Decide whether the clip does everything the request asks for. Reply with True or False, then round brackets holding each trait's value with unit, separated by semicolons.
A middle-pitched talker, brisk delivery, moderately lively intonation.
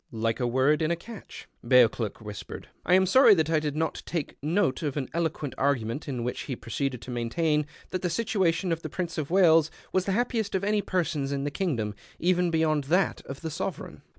True (155 Hz; 210 wpm; 4.9 semitones)